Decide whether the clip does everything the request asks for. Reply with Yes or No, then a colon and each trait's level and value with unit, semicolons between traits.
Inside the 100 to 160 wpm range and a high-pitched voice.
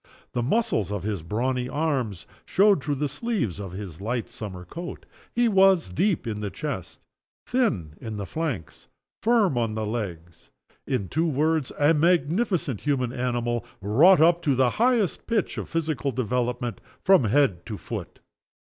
No: average, 155 wpm; low, 130 Hz